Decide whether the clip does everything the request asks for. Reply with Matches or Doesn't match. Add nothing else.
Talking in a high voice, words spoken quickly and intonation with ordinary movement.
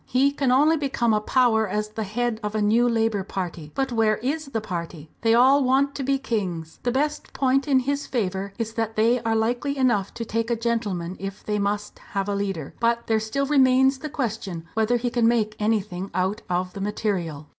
Matches